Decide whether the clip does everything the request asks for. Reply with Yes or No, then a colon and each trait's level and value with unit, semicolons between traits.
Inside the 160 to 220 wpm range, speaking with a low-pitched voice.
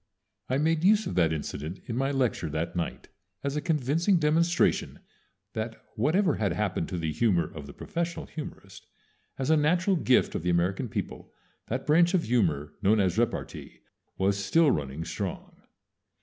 Yes: average, 170 wpm; low, 120 Hz